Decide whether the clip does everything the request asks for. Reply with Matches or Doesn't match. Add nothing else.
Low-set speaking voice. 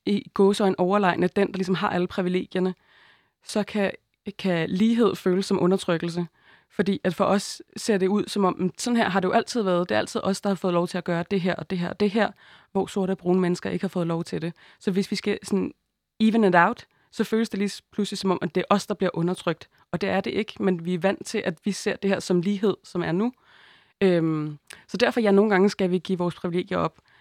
Doesn't match